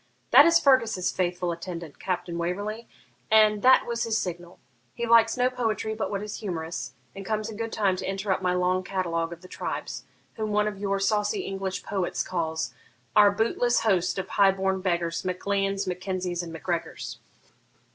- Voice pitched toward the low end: No, high, 195 Hz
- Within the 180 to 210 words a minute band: Yes, average, 185 wpm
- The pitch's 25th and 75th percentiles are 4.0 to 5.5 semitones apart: No, average, 3.1 semitones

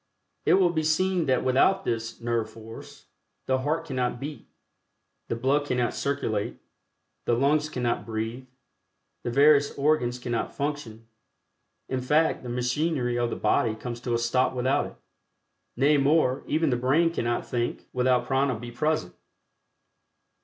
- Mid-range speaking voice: No, low, 130 Hz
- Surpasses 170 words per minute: No, average, 145 wpm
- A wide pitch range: No, average, 3.7 semitones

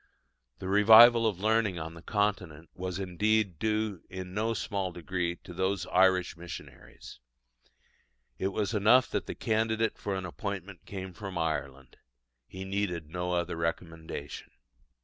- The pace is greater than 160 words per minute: No, average, 140 wpm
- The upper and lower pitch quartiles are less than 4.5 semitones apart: Yes, average, 3.3 semitones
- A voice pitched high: No, very low, 95 Hz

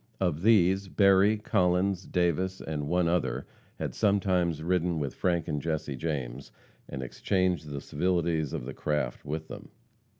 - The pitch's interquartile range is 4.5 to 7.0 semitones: No, average, 3.7 semitones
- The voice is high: No, very low, 85 Hz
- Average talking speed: Yes, average, 145 wpm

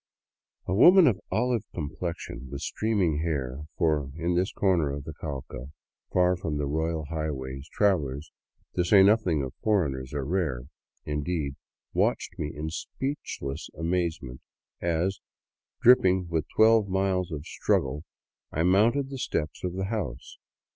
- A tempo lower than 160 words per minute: Yes, average, 145 wpm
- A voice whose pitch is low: Yes, very low, 85 Hz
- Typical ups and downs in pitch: Yes, average, 4.7 semitones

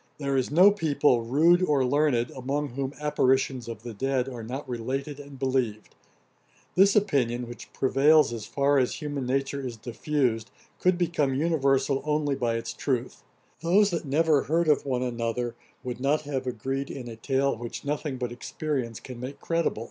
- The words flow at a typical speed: Yes, average, 170 wpm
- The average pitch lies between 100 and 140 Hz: Yes, low, 135 Hz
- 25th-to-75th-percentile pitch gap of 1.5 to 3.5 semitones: Yes, average, 3.2 semitones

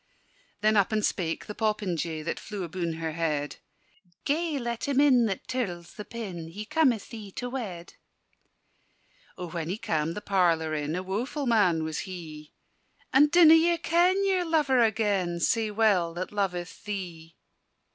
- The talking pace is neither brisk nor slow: Yes, average, 160 wpm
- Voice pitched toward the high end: Yes, high, 205 Hz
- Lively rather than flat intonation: Yes, wide, 6.2 semitones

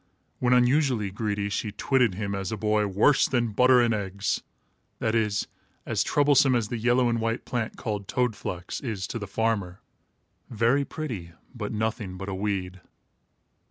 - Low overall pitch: Yes, low, 110 Hz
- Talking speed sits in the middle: Yes, average, 165 wpm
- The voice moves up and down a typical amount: Yes, average, 3.4 semitones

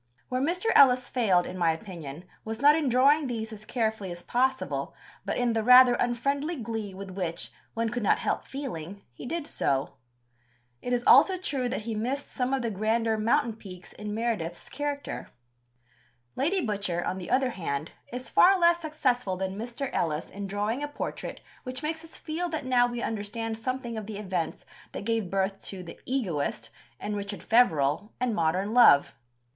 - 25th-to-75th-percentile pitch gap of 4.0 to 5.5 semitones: Yes, average, 5.0 semitones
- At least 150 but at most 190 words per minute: Yes, average, 180 wpm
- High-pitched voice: Yes, high, 230 Hz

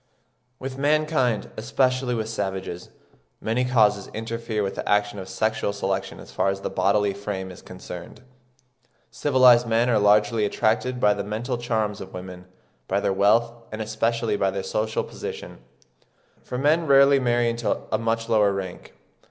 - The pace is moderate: Yes, average, 160 wpm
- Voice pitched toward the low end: Yes, low, 110 Hz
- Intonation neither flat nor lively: Yes, average, 3.2 semitones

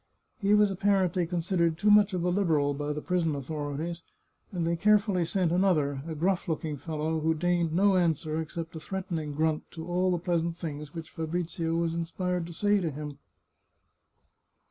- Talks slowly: No, average, 175 wpm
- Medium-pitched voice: Yes, medium, 170 Hz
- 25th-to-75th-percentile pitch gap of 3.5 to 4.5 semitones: No, narrow, 2.4 semitones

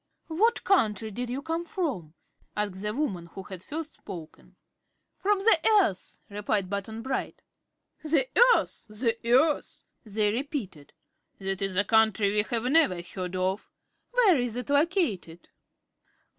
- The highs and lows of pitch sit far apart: Yes, wide, 7.5 semitones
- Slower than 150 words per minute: Yes, average, 140 wpm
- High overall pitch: Yes, high, 220 Hz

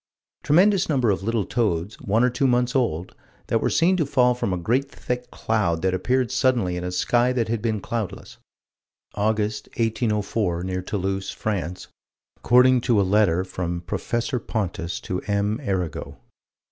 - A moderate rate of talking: Yes, average, 160 wpm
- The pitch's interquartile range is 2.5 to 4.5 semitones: No, average, 4.9 semitones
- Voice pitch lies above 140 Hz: No, low, 110 Hz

